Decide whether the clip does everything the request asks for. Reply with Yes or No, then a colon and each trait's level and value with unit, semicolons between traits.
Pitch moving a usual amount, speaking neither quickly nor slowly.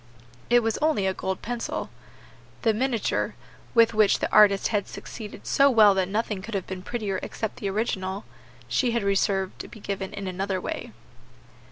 Yes: average, 3.0 semitones; average, 180 wpm